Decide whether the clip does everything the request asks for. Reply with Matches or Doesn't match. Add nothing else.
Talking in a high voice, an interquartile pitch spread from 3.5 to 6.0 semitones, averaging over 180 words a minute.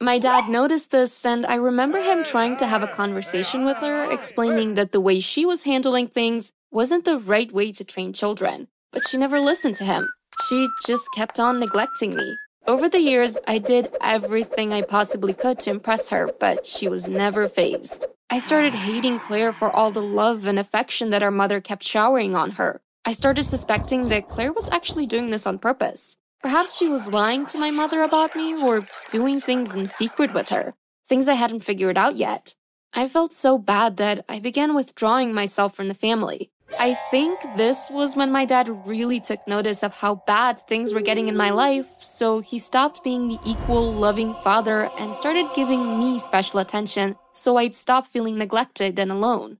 Matches